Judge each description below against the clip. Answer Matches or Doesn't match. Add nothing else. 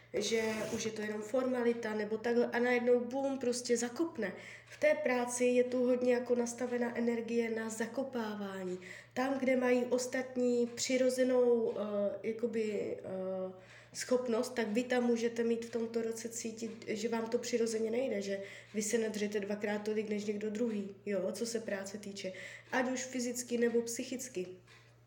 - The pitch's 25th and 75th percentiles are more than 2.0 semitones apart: Matches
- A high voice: Matches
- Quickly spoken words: Doesn't match